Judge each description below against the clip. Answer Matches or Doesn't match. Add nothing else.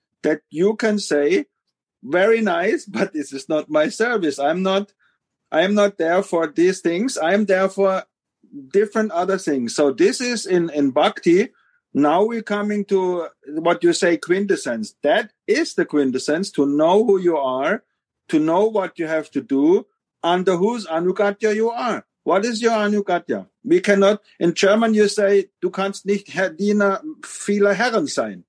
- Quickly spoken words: Doesn't match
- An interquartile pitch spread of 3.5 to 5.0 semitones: Matches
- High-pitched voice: Matches